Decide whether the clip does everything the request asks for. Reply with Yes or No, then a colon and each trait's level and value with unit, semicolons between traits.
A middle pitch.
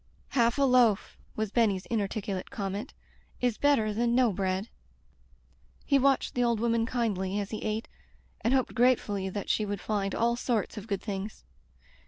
No: high, 220 Hz